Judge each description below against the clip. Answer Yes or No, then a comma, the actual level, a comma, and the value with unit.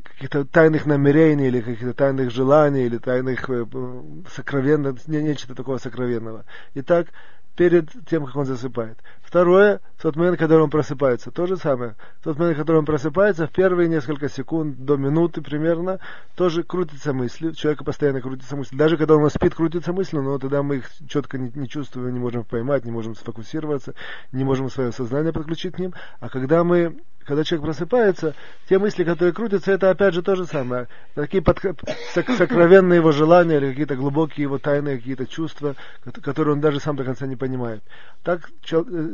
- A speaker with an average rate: No, fast, 180 wpm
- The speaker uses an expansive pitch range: No, average, 4.2 semitones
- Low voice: No, medium, 150 Hz